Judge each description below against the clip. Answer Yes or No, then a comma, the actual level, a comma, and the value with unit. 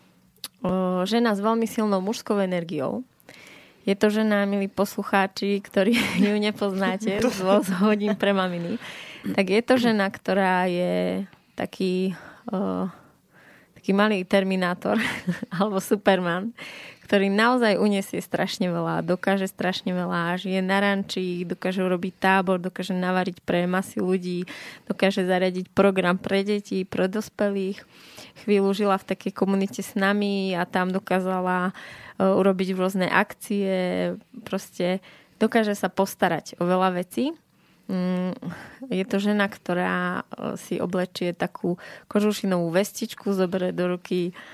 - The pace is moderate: Yes, average, 120 wpm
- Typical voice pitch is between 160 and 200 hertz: Yes, high, 190 Hz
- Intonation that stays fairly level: Yes, narrow, 2.0 semitones